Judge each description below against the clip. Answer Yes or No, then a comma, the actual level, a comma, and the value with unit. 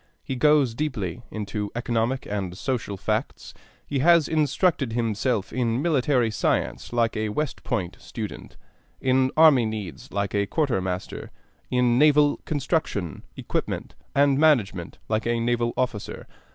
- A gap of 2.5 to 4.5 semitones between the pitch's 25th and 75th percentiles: No, average, 5.0 semitones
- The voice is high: No, low, 120 Hz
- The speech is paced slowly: Yes, slow, 130 wpm